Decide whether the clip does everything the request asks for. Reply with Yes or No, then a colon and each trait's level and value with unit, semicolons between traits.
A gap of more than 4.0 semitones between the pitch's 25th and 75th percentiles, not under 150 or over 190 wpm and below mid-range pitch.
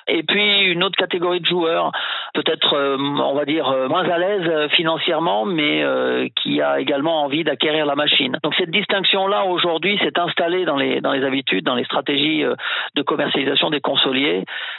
No: average, 4.5 semitones; average, 160 wpm; medium, 165 Hz